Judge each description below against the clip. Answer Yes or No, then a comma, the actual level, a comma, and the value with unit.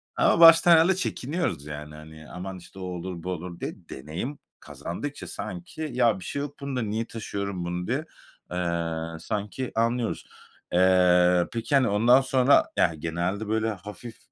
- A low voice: Yes, low, 100 Hz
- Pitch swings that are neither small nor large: No, wide, 6.5 semitones